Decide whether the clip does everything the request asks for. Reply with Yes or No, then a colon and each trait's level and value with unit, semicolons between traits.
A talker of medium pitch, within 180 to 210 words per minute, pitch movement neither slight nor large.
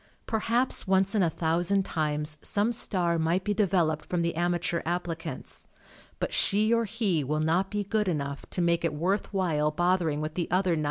Yes: medium, 175 Hz; average, 195 wpm; average, 3.5 semitones